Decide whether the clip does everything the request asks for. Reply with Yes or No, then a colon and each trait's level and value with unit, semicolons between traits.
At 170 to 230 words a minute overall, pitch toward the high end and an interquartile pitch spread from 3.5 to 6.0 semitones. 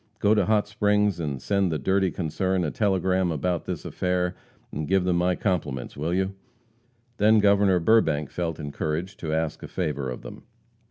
No: average, 175 wpm; very low, 90 Hz; average, 3.8 semitones